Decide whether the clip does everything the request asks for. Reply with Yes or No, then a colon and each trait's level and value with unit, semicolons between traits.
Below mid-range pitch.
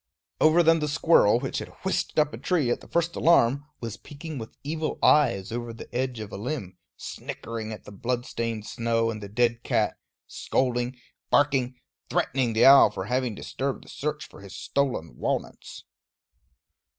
Yes: low, 125 Hz